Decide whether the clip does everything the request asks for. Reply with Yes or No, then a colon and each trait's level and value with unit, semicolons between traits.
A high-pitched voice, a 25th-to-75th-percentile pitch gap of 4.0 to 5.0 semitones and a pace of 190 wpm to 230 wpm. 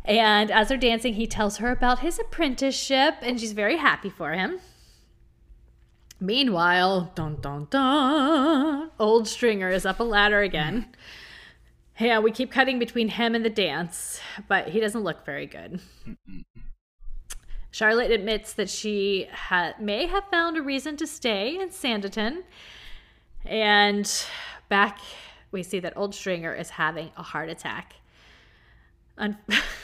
No: high, 220 Hz; average, 4.4 semitones; average, 140 wpm